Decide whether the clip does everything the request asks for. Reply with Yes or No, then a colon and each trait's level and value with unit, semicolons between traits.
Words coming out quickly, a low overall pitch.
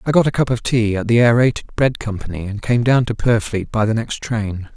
Yes: fast, 250 wpm; low, 115 Hz